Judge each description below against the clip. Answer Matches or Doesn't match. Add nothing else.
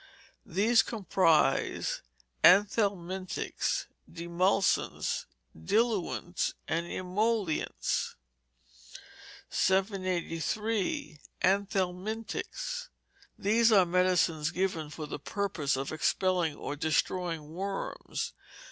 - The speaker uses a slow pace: Matches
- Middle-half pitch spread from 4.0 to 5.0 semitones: Doesn't match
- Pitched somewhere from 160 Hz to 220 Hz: Matches